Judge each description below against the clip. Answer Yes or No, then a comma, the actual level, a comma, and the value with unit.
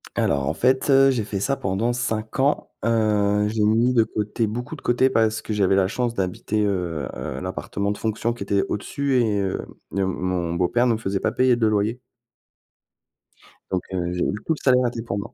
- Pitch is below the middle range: Yes, low, 110 Hz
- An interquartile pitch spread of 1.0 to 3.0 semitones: No, average, 3.7 semitones